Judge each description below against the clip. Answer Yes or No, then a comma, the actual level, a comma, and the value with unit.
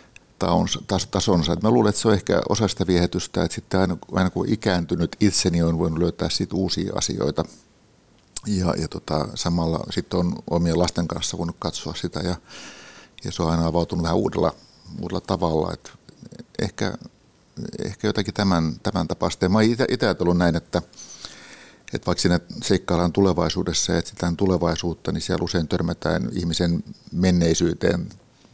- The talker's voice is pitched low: Yes, very low, 90 Hz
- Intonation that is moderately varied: No, narrow, 2.0 semitones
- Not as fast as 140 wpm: No, average, 145 wpm